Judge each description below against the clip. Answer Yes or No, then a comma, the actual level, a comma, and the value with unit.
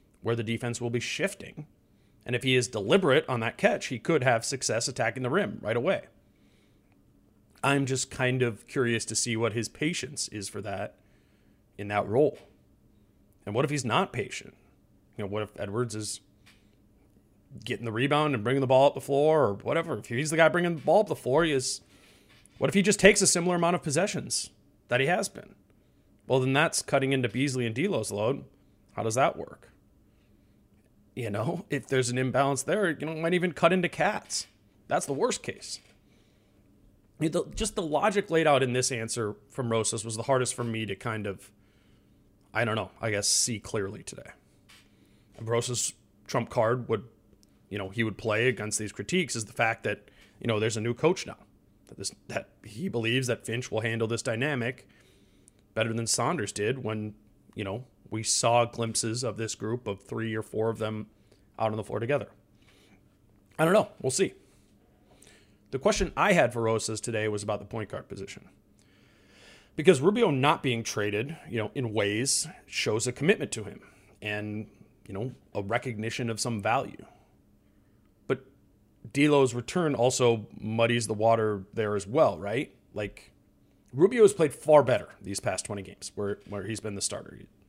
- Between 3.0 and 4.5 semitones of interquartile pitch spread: Yes, average, 4.2 semitones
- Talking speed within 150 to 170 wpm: No, average, 185 wpm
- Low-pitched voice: Yes, low, 115 Hz